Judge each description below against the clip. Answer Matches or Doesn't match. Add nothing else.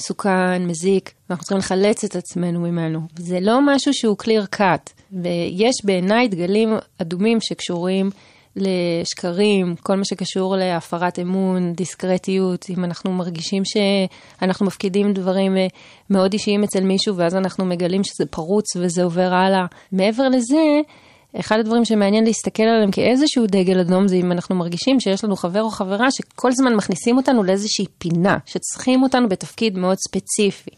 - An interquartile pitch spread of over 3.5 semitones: Doesn't match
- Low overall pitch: Doesn't match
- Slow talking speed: Doesn't match